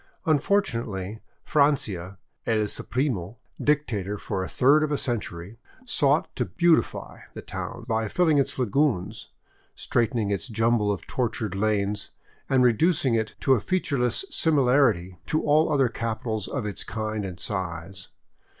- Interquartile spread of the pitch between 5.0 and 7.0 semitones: Yes, wide, 5.5 semitones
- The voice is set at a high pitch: No, low, 115 Hz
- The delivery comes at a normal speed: Yes, average, 150 wpm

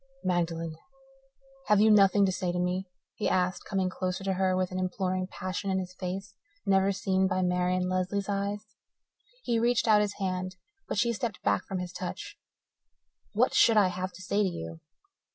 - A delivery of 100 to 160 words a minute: No, average, 185 wpm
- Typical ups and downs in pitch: No, narrow, 1.7 semitones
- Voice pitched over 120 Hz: Yes, medium, 185 Hz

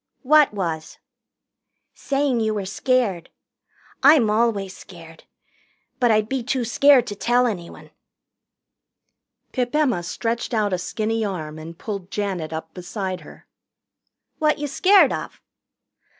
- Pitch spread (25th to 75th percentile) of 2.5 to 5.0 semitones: No, wide, 5.5 semitones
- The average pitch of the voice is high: Yes, high, 215 Hz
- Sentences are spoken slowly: Yes, slow, 125 wpm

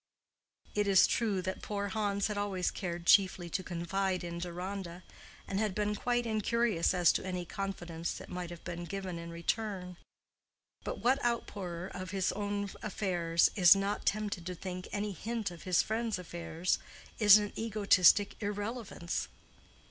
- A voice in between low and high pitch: No, high, 195 Hz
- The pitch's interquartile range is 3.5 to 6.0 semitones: No, average, 2.9 semitones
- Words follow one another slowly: No, average, 155 wpm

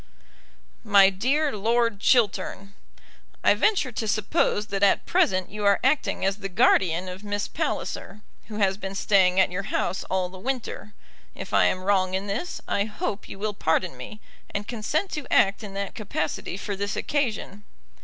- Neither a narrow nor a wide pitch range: No, narrow, 2.2 semitones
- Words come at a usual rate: Yes, average, 175 wpm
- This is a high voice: Yes, high, 200 Hz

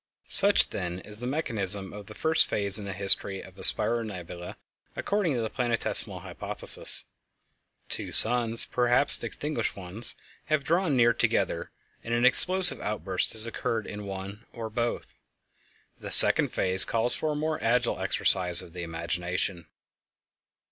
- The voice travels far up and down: No, average, 4.3 semitones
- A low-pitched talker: Yes, low, 110 Hz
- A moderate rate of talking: Yes, average, 150 wpm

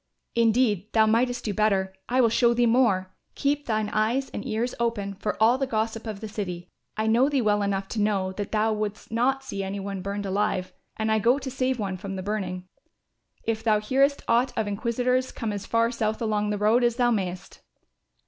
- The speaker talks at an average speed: No, fast, 210 wpm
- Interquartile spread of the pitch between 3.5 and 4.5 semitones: No, average, 3.0 semitones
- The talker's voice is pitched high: Yes, high, 220 Hz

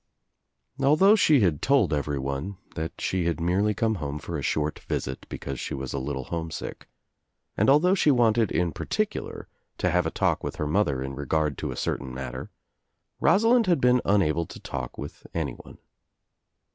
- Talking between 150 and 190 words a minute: Yes, average, 170 wpm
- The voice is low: Yes, very low, 85 Hz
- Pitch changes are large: Yes, wide, 8.8 semitones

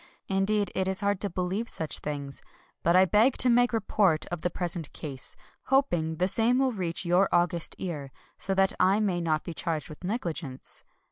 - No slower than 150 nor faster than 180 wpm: No, average, 195 wpm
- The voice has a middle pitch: Yes, medium, 180 Hz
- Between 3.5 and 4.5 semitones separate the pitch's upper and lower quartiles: Yes, average, 3.8 semitones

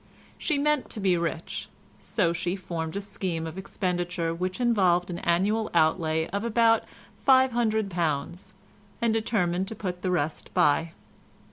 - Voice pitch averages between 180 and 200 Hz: Yes, medium, 185 Hz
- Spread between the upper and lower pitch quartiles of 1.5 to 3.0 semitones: No, average, 4.2 semitones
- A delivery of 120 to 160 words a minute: Yes, average, 140 wpm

